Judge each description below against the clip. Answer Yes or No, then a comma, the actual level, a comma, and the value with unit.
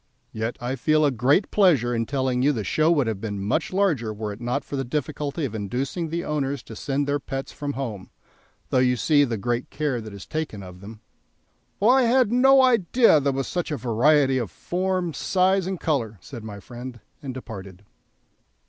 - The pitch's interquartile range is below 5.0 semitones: No, wide, 5.5 semitones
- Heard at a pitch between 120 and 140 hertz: Yes, low, 135 Hz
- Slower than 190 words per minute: No, average, 200 wpm